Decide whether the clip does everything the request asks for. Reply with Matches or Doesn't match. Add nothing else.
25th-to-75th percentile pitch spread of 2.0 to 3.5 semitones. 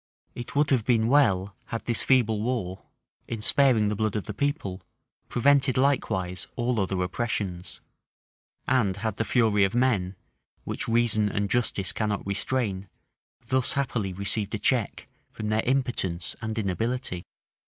Doesn't match